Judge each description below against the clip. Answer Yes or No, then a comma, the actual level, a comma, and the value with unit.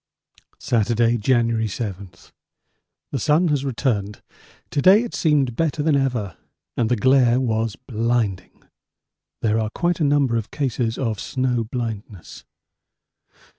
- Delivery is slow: Yes, slow, 130 wpm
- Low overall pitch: Yes, low, 120 Hz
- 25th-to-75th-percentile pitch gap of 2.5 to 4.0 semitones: Yes, average, 3.7 semitones